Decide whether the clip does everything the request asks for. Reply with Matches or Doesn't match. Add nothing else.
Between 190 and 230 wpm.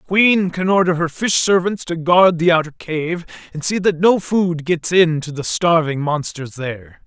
Matches